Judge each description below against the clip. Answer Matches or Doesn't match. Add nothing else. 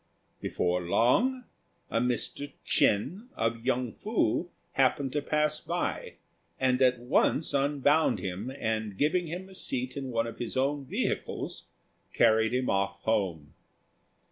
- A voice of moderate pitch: Doesn't match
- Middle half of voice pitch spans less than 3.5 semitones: Doesn't match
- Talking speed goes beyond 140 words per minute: Doesn't match